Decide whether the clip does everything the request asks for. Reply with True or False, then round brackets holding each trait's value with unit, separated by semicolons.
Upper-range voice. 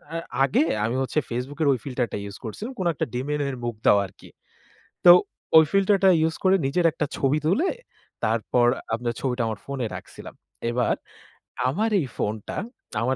False (135 Hz)